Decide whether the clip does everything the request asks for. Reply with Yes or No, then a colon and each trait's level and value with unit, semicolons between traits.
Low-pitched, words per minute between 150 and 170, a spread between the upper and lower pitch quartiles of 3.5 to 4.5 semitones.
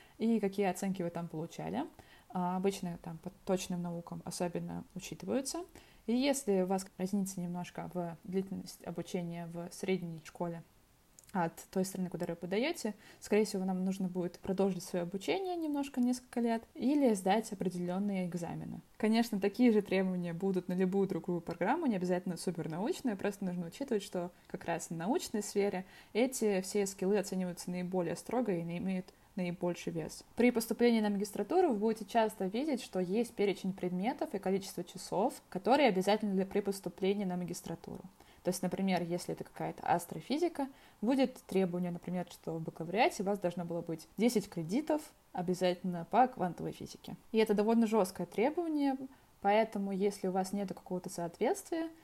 No: high, 190 Hz; fast, 160 wpm; average, 3.8 semitones